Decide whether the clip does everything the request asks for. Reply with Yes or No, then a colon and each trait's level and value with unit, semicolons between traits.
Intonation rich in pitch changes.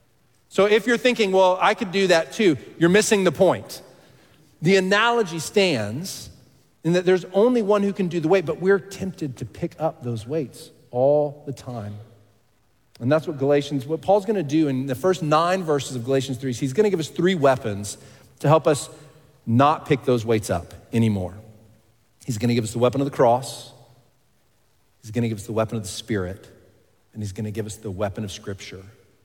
Yes: wide, 7.1 semitones